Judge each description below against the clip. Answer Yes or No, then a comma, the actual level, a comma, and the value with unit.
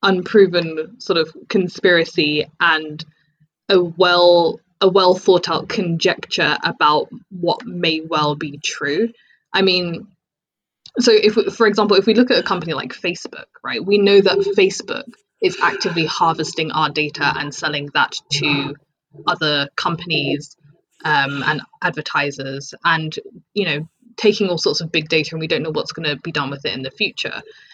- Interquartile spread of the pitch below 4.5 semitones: No, average, 4.8 semitones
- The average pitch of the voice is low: No, medium, 170 Hz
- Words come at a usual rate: Yes, average, 160 wpm